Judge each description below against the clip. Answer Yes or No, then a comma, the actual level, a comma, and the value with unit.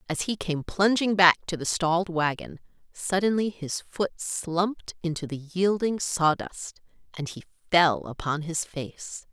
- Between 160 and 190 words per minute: No, average, 150 wpm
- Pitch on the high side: No, medium, 175 Hz